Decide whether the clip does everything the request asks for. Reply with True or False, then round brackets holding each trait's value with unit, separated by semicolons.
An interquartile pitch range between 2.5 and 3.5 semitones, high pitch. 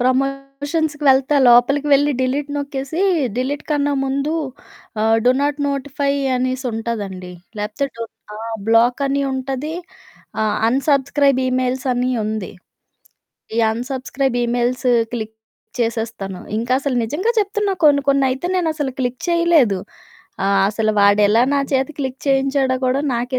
True (2.9 semitones; 265 Hz)